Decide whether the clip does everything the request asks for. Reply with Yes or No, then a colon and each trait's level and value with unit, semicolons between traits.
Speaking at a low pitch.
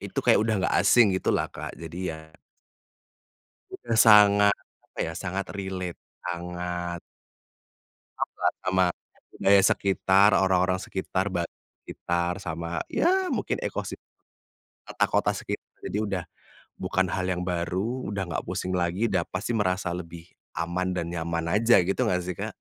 Yes: very low, 90 Hz